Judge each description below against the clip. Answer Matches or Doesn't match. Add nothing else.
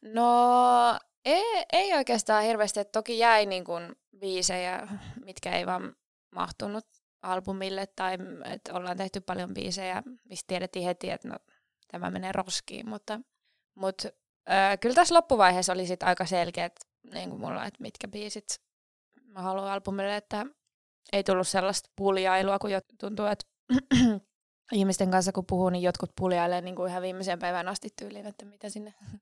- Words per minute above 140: Matches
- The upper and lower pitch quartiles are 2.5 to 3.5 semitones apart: Matches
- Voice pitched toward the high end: Matches